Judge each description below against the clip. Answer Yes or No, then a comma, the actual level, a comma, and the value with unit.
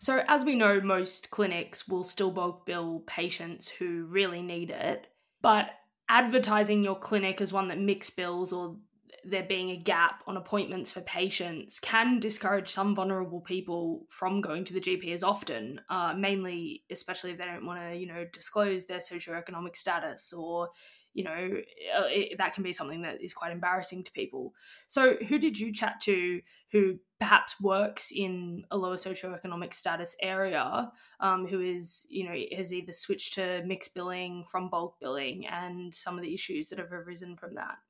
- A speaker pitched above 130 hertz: Yes, medium, 185 Hz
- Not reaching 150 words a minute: No, average, 175 wpm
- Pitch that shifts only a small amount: Yes, narrow, 2.1 semitones